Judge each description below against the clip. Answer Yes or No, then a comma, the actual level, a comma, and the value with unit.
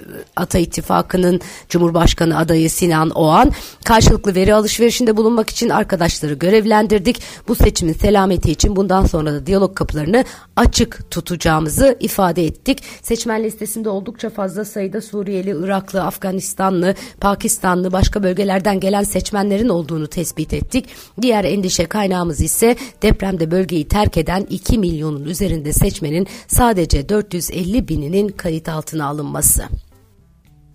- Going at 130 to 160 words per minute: No, average, 115 wpm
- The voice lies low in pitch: No, high, 190 Hz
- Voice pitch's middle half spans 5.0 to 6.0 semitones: No, average, 4.2 semitones